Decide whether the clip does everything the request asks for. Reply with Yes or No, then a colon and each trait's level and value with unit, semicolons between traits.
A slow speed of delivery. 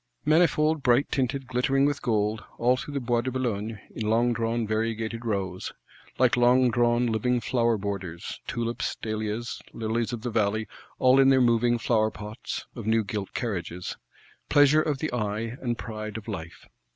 No: average, 155 wpm